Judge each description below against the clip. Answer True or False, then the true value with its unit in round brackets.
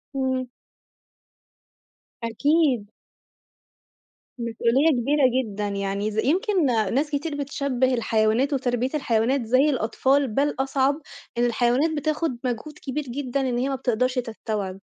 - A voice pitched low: False (255 Hz)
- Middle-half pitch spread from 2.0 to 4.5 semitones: True (3.6 semitones)